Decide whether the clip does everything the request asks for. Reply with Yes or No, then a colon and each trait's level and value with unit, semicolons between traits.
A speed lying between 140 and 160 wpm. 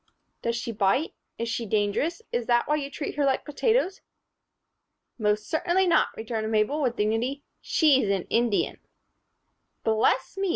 Yes: average, 150 wpm